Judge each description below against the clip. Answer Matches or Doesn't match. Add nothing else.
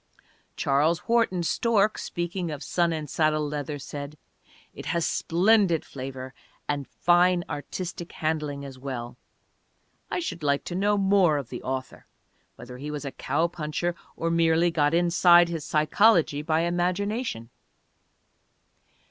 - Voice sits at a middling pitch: Matches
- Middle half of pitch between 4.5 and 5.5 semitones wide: Doesn't match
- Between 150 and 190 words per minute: Doesn't match